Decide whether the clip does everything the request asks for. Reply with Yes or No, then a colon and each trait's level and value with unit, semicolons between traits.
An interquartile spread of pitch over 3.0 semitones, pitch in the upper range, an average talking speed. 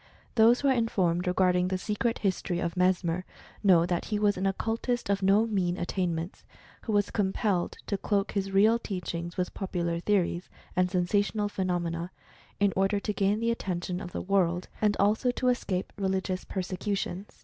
No: narrow, 2.5 semitones; high, 195 Hz; average, 170 wpm